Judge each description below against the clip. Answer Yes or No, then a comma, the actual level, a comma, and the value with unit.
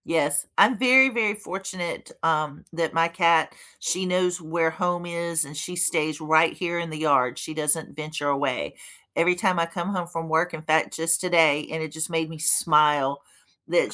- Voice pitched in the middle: Yes, medium, 165 Hz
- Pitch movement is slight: Yes, narrow, 2.3 semitones